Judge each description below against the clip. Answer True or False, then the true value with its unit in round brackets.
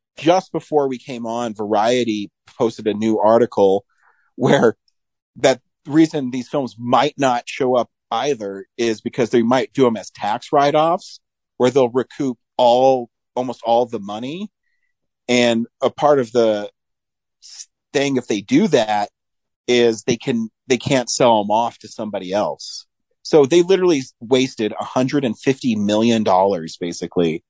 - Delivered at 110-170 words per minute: True (140 wpm)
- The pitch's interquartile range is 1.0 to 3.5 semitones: False (4.2 semitones)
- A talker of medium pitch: False (125 Hz)